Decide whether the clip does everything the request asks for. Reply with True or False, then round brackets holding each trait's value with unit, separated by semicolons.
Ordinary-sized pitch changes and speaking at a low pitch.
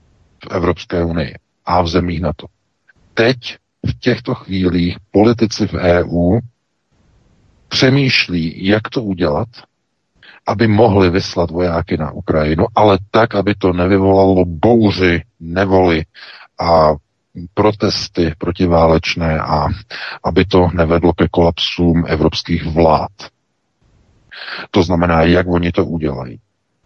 True (3.3 semitones; 90 Hz)